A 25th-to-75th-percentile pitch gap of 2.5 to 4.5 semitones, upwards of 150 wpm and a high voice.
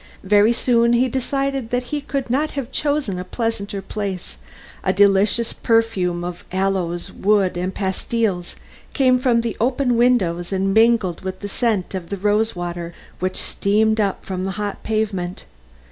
Yes: average, 4.0 semitones; average, 160 wpm; high, 205 Hz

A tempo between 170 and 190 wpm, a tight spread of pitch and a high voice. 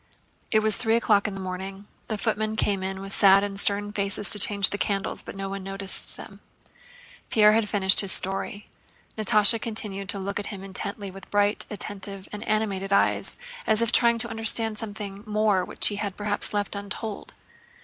Yes: average, 185 wpm; narrow, 1.5 semitones; high, 205 Hz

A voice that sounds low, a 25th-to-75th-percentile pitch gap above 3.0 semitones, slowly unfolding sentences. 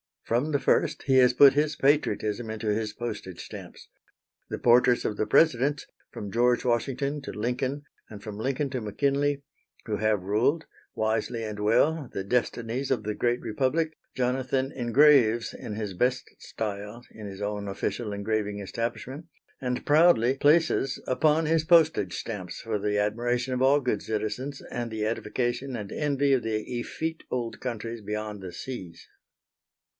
No: low, 120 Hz; average, 4.3 semitones; average, 155 wpm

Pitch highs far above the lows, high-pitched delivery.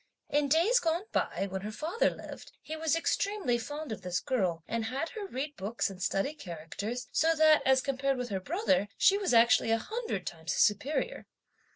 Yes: wide, 7.3 semitones; very high, 260 Hz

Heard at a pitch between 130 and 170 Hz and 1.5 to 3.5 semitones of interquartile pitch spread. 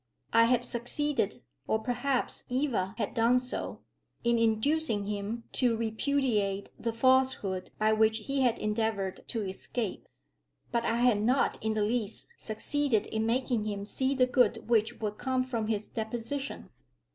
No: high, 230 Hz; average, 2.8 semitones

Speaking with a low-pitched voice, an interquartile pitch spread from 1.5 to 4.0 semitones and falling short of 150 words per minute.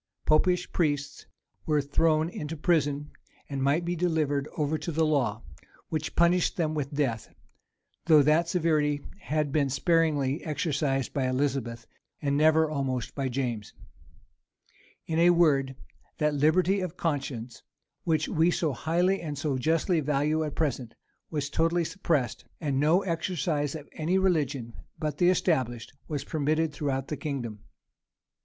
No: medium, 150 Hz; average, 2.9 semitones; average, 140 wpm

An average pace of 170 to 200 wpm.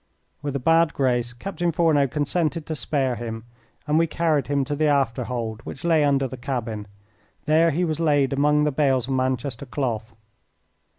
Yes: average, 180 wpm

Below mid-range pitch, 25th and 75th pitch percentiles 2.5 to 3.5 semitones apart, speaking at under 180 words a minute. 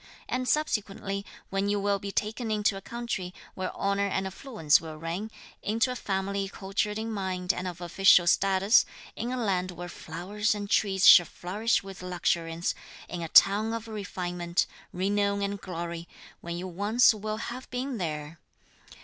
No: high, 195 Hz; average, 3.0 semitones; average, 165 wpm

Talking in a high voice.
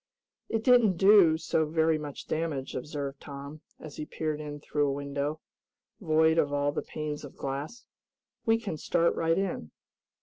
No: medium, 155 Hz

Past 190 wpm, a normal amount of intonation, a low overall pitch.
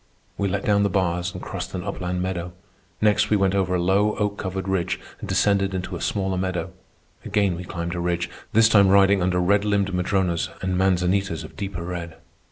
No: average, 200 wpm; narrow, 1.9 semitones; very low, 95 Hz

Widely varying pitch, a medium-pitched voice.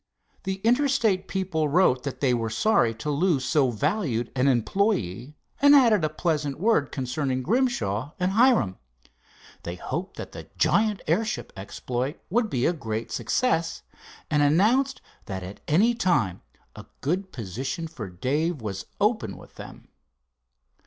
Yes: wide, 8.5 semitones; medium, 150 Hz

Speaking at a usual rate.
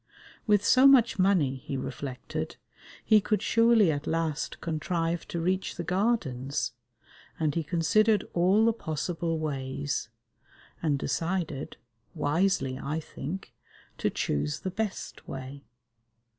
No: slow, 120 wpm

